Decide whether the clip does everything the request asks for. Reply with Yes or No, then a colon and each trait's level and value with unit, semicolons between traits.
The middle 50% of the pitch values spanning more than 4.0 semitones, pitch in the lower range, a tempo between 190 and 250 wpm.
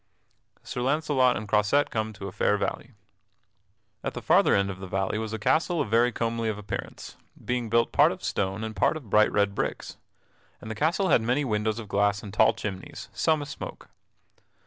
No: average, 3.3 semitones; low, 110 Hz; fast, 205 wpm